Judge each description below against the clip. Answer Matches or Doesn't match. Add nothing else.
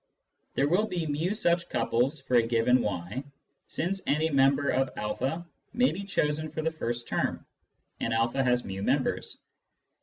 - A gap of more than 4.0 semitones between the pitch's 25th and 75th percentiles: Matches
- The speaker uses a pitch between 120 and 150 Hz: Matches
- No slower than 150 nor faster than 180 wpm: Matches